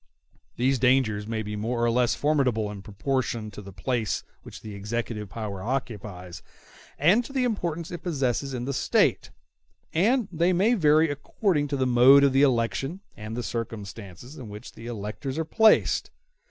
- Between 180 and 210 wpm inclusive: No, average, 165 wpm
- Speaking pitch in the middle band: No, low, 125 Hz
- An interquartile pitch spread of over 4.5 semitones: Yes, wide, 5.6 semitones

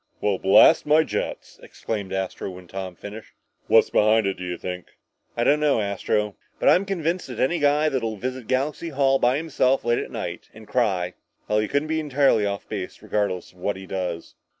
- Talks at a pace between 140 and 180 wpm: No, average, 200 wpm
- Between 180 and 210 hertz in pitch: No, low, 110 Hz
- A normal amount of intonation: No, wide, 6.7 semitones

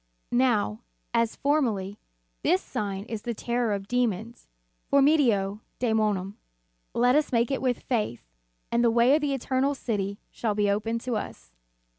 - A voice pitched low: No, high, 230 Hz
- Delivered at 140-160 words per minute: Yes, average, 150 wpm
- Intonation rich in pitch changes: No, average, 3.5 semitones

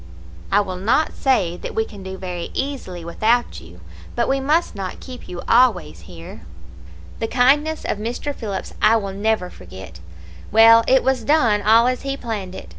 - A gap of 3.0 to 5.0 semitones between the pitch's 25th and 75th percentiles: No, wide, 5.6 semitones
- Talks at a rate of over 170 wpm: Yes, average, 180 wpm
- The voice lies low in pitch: No, high, 220 Hz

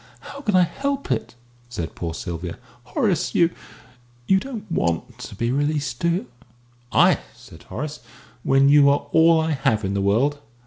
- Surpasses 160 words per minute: Yes, average, 170 wpm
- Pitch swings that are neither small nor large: No, wide, 7.2 semitones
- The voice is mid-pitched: Yes, medium, 145 Hz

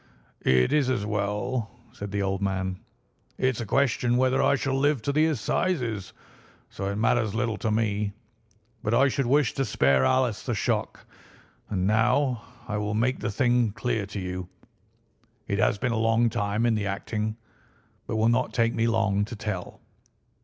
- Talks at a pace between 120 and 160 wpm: No, average, 175 wpm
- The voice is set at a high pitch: No, low, 110 Hz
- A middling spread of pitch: Yes, average, 3.5 semitones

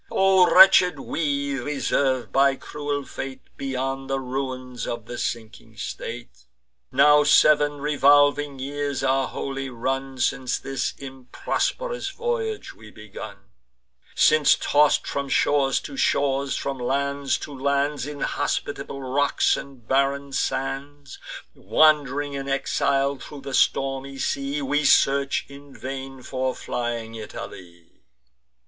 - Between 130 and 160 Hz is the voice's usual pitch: Yes, low, 135 Hz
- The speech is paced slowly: Yes, slow, 115 wpm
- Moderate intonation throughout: No, narrow, 1.6 semitones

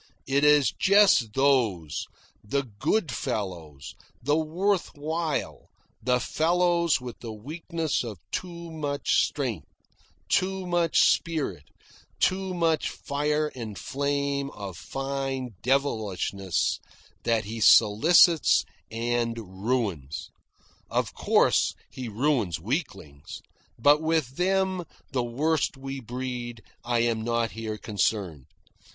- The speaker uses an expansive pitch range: Yes, wide, 6.2 semitones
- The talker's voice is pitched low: Yes, low, 130 Hz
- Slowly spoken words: Yes, slow, 110 wpm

